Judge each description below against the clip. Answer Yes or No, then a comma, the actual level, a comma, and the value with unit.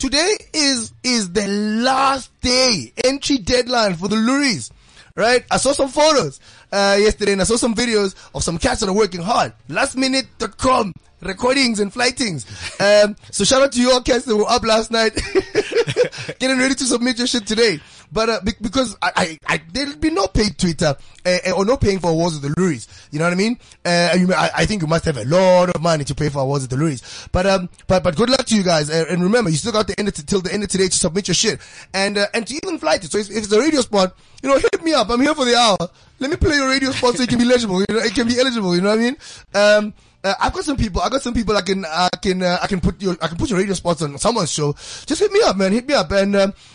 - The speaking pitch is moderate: No, high, 210 Hz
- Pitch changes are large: Yes, wide, 5.7 semitones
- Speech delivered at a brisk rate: Yes, fast, 270 wpm